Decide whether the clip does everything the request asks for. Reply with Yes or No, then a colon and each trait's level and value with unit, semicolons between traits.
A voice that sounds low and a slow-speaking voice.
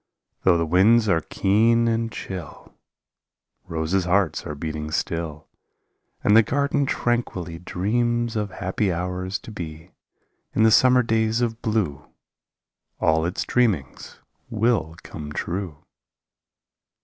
Yes: very low, 95 Hz; slow, 125 wpm